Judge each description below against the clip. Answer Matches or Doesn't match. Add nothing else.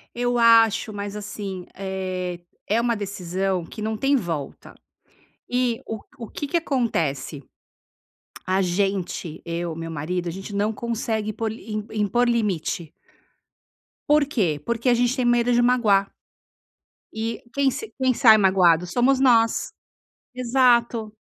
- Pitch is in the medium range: Doesn't match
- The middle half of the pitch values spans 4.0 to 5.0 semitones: Matches